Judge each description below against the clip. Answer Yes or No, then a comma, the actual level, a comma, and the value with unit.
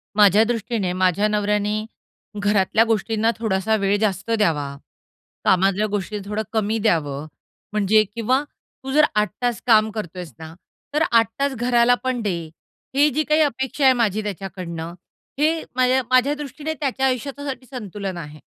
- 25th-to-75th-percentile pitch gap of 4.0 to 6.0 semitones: Yes, average, 4.6 semitones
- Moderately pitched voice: No, high, 215 Hz